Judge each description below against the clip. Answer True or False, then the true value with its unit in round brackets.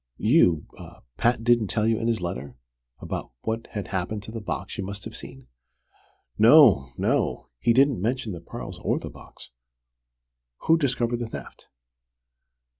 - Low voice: True (110 Hz)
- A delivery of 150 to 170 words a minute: True (155 wpm)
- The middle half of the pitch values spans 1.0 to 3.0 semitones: False (4.2 semitones)